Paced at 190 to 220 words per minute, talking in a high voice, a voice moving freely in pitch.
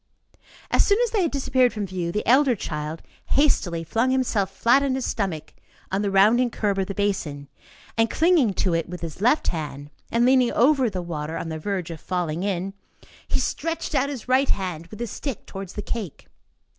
Yes: average, 200 wpm; high, 205 Hz; wide, 6.9 semitones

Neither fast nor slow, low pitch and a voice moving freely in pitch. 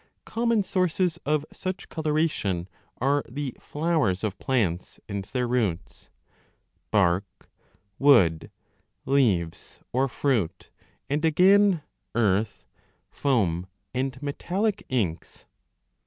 No: slow, 95 wpm; low, 130 Hz; wide, 8.0 semitones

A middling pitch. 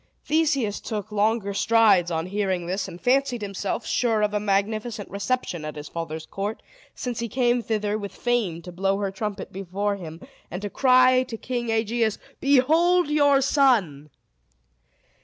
No: high, 210 Hz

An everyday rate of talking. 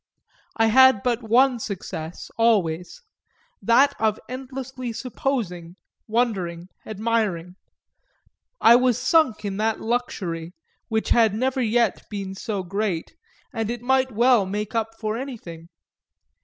No: slow, 120 wpm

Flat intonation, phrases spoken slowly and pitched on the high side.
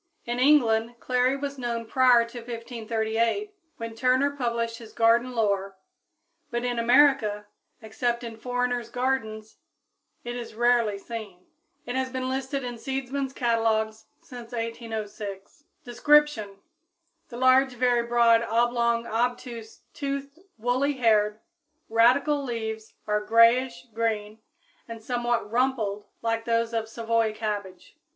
Yes: narrow, 2.1 semitones; slow, 120 wpm; high, 235 Hz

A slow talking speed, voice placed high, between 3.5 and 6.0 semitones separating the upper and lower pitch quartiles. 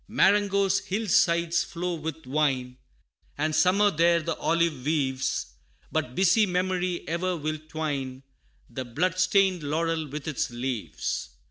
No: slow, 130 wpm; medium, 165 Hz; average, 4.0 semitones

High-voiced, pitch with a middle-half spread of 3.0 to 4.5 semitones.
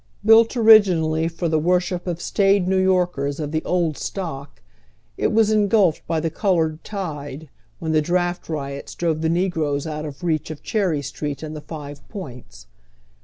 No: medium, 165 Hz; average, 3.5 semitones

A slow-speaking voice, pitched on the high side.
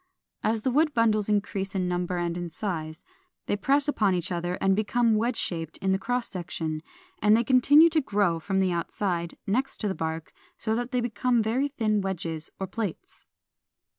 No: average, 185 wpm; high, 205 Hz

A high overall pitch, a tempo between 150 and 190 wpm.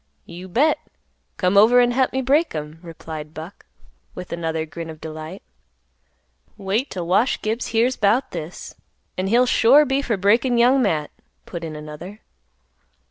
Yes: high, 195 Hz; average, 155 wpm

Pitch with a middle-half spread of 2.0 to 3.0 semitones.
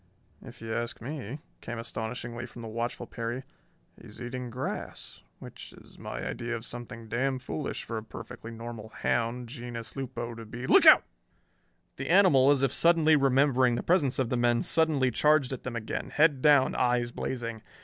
Yes: narrow, 2.6 semitones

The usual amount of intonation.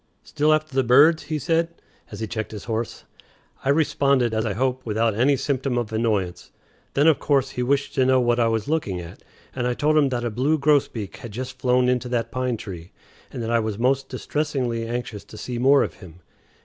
Yes: average, 3.5 semitones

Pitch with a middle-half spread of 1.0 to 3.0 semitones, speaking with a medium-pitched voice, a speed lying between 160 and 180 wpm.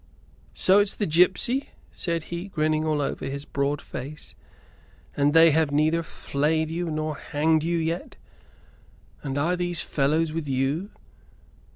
No: narrow, 2.4 semitones; medium, 155 Hz; average, 145 wpm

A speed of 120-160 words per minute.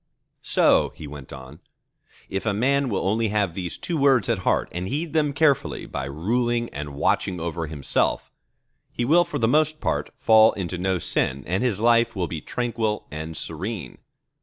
No: average, 180 wpm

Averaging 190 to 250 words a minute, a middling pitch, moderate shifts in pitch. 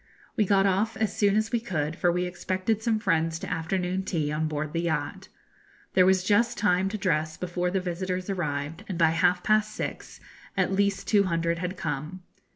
Yes: average, 200 wpm; medium, 180 Hz; average, 3.1 semitones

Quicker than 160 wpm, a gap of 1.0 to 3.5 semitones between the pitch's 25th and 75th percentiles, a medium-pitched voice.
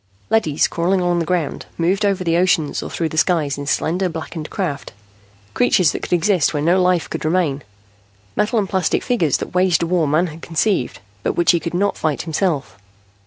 Yes: average, 200 wpm; average, 2.9 semitones; medium, 170 Hz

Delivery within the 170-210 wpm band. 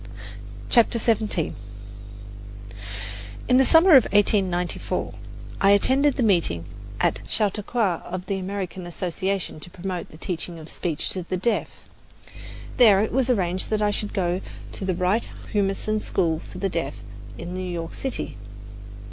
No: average, 145 wpm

